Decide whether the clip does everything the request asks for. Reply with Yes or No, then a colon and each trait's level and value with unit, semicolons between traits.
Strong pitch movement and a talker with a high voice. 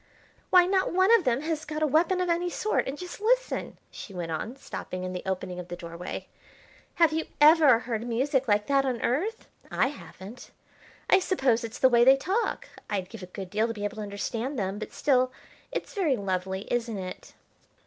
Yes: wide, 7.7 semitones; very high, 250 Hz